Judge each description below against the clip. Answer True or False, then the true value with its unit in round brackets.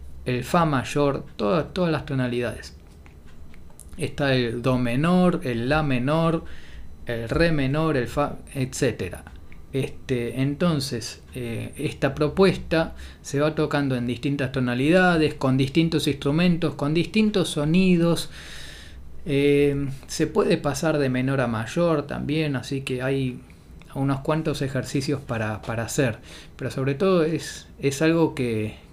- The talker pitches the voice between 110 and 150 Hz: True (140 Hz)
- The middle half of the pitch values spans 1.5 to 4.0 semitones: False (4.5 semitones)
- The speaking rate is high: False (130 wpm)